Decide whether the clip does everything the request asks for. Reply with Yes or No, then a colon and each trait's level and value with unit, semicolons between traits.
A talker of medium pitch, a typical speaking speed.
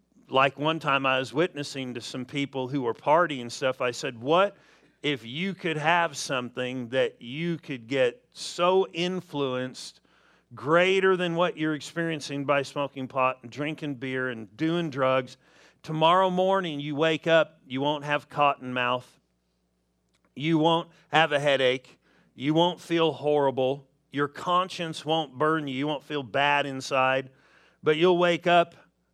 Yes: medium, 145 Hz; average, 155 wpm